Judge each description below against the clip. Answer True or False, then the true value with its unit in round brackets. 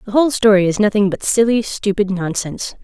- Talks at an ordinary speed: True (190 wpm)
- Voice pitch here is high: True (205 Hz)